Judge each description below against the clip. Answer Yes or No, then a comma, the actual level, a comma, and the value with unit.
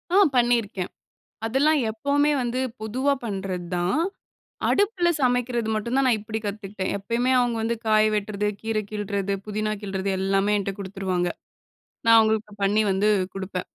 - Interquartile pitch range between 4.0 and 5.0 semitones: No, average, 3.4 semitones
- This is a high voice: Yes, high, 215 Hz